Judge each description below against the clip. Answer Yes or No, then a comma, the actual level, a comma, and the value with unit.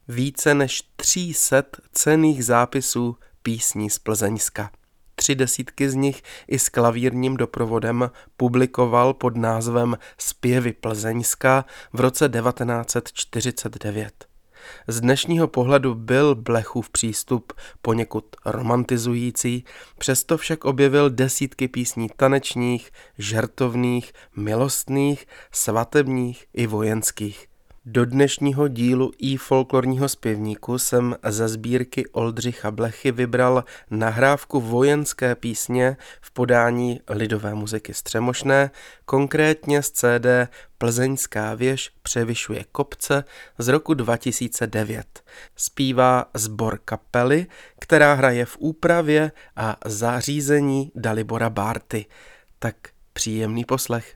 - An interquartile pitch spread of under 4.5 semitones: Yes, average, 2.8 semitones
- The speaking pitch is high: No, low, 125 Hz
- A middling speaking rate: No, slow, 100 wpm